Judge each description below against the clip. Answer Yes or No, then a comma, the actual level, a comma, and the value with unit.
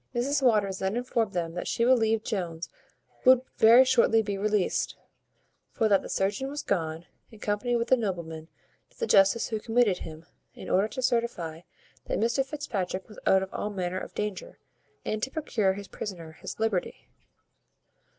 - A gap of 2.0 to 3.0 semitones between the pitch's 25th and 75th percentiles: No, average, 4.1 semitones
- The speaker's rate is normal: Yes, average, 170 wpm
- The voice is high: Yes, high, 210 Hz